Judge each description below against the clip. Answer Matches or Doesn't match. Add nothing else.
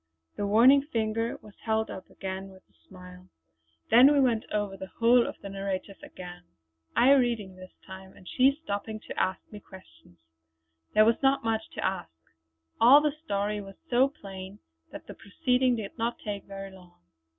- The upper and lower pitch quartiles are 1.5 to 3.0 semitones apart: Doesn't match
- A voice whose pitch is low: Doesn't match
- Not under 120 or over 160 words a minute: Doesn't match